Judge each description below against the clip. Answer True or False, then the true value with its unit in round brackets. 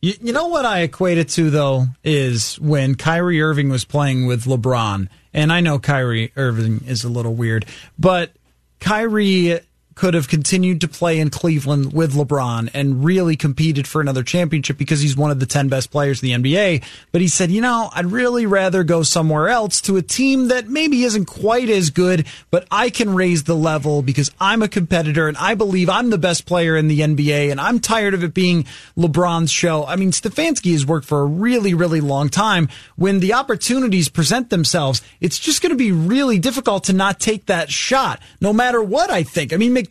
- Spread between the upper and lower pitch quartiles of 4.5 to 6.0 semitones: True (5.4 semitones)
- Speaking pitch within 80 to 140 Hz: False (170 Hz)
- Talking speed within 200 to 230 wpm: True (205 wpm)